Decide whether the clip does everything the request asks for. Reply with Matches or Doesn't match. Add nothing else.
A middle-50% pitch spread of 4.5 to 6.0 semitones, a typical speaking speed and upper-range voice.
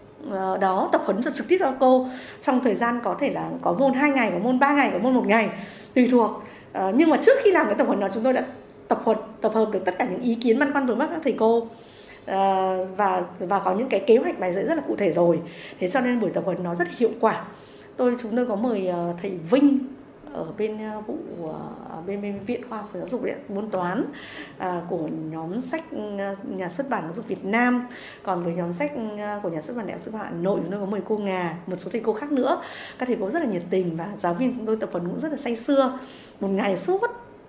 Doesn't match